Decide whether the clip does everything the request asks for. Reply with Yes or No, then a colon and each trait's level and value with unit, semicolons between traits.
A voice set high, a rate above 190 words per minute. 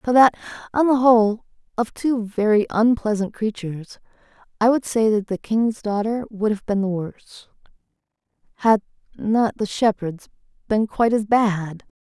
No: high, 215 Hz; average, 150 wpm